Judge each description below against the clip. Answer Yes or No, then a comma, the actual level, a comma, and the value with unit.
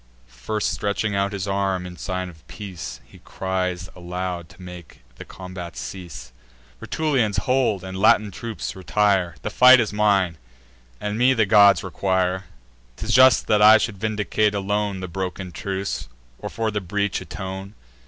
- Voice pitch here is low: Yes, very low, 95 Hz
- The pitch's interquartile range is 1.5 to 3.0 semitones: Yes, narrow, 2.5 semitones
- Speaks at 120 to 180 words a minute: Yes, average, 155 wpm